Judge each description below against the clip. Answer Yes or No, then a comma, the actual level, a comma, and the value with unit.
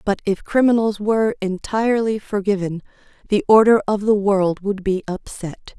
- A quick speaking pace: No, average, 145 wpm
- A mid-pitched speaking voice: No, high, 205 Hz